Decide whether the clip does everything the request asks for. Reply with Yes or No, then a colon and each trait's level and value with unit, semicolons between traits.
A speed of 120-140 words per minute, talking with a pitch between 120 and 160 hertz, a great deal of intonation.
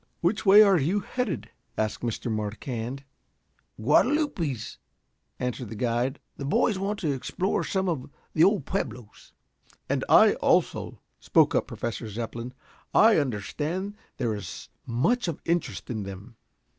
Yes: slow, 135 wpm; low, 135 Hz; wide, 8.5 semitones